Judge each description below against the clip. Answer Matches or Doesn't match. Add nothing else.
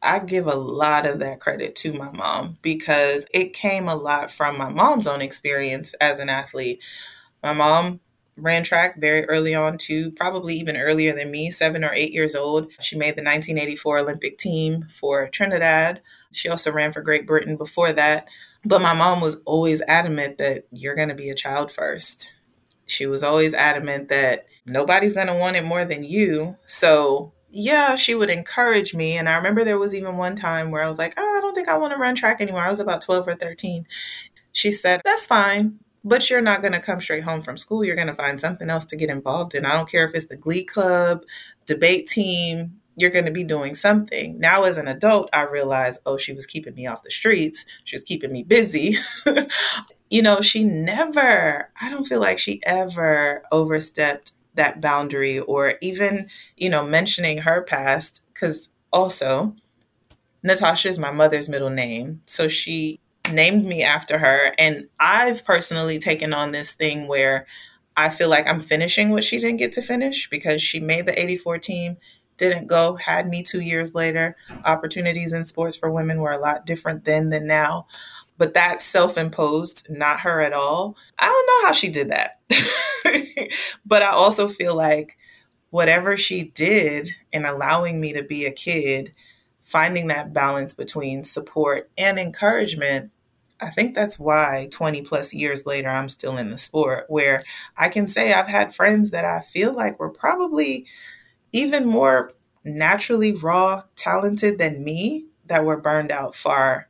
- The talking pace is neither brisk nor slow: Matches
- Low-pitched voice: Doesn't match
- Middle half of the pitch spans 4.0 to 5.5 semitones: Matches